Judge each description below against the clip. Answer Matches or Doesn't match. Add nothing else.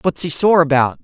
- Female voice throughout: Doesn't match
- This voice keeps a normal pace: Doesn't match